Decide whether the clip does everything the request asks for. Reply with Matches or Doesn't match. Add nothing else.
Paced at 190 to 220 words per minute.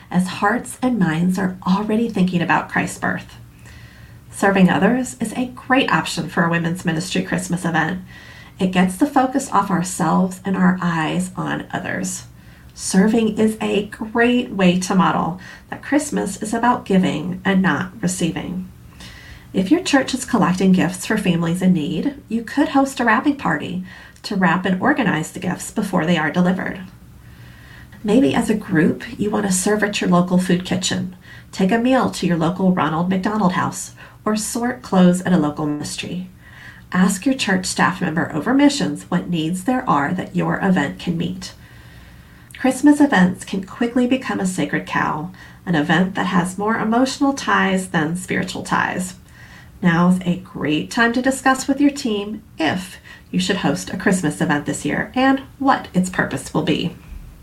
Doesn't match